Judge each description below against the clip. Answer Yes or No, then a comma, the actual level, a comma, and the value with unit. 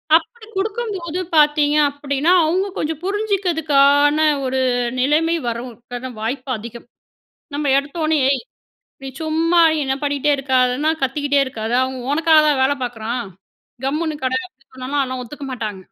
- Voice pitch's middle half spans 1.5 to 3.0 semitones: No, average, 3.6 semitones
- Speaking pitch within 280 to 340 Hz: Yes, very high, 285 Hz